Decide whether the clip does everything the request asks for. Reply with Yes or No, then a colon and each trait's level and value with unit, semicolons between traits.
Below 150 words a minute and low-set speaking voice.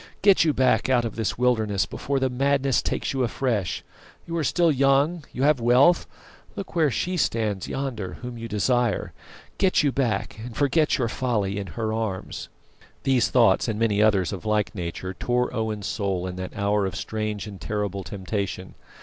No: average, 180 wpm; low, 115 Hz